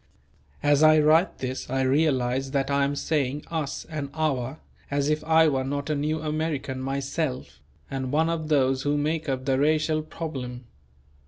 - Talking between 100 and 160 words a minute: No, average, 170 wpm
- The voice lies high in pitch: No, medium, 145 Hz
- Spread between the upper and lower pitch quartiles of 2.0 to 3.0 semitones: Yes, average, 2.7 semitones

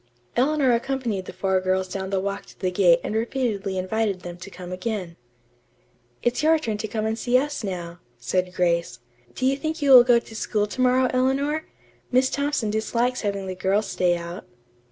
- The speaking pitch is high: Yes, high, 215 Hz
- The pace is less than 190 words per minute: No, average, 195 wpm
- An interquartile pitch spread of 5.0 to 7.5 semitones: Yes, wide, 5.5 semitones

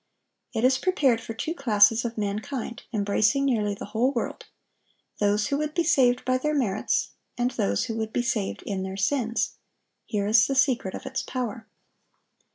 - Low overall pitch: No, high, 230 Hz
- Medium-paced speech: Yes, average, 170 wpm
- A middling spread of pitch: Yes, average, 3.9 semitones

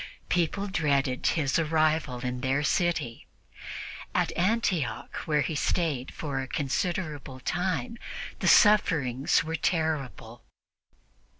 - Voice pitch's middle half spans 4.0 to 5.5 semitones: Yes, average, 4.5 semitones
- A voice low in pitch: No, medium, 155 Hz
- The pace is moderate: No, slow, 105 wpm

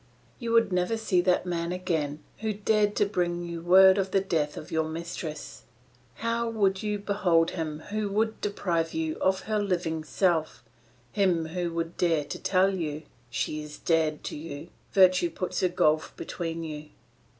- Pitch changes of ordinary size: Yes, average, 3.5 semitones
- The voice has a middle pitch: Yes, medium, 175 Hz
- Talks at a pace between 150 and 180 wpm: Yes, average, 170 wpm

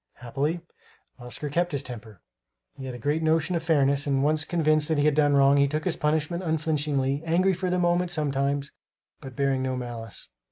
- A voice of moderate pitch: Yes, medium, 150 Hz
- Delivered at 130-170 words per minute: No, average, 195 wpm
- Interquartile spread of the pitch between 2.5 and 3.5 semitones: Yes, average, 2.9 semitones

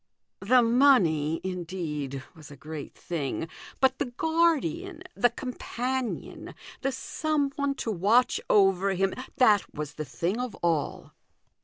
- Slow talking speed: Yes, slow, 130 wpm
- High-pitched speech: Yes, high, 210 Hz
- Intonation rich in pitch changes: Yes, wide, 8.2 semitones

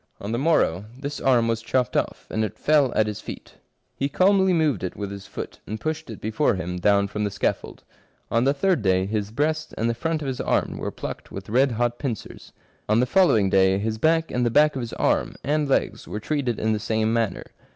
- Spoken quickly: Yes, fast, 230 wpm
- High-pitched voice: No, low, 115 Hz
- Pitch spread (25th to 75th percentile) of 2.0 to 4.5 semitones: No, wide, 5.5 semitones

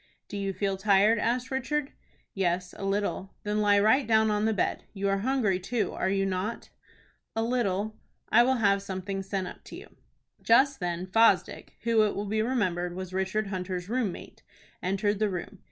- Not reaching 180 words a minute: No, average, 185 wpm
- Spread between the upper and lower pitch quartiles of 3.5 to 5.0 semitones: No, average, 2.8 semitones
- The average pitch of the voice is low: No, high, 205 Hz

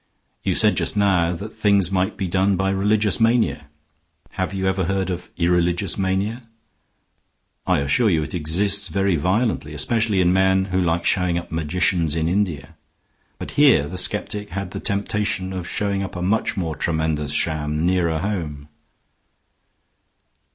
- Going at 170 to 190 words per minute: No, average, 155 wpm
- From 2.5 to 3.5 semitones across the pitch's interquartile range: Yes, average, 3.0 semitones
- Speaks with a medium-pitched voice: No, very low, 95 Hz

